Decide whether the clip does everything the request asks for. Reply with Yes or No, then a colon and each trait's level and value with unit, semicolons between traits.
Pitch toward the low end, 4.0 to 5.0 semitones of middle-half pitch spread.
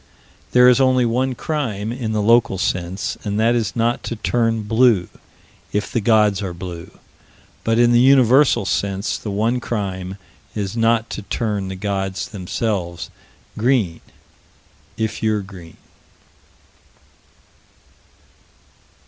No: low, 110 Hz; average, 3.4 semitones